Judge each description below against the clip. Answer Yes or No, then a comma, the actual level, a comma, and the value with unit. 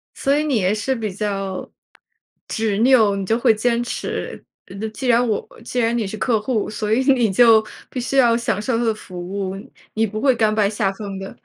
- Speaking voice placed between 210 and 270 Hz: Yes, high, 220 Hz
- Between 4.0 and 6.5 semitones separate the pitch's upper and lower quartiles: No, average, 2.8 semitones